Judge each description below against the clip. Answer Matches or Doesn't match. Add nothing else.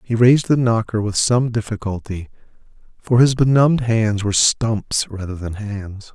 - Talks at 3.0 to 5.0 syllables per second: Matches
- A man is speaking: Matches